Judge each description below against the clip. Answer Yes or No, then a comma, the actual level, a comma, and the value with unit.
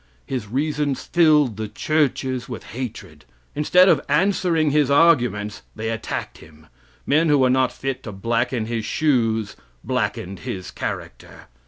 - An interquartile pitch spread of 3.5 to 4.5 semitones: No, average, 5.2 semitones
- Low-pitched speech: Yes, low, 130 Hz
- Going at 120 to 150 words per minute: Yes, average, 140 wpm